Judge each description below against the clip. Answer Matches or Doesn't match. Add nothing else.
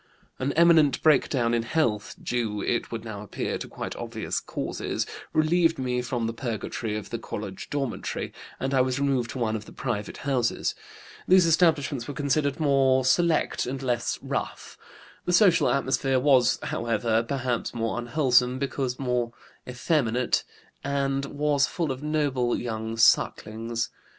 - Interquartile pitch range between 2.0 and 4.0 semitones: Matches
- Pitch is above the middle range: Doesn't match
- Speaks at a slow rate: Doesn't match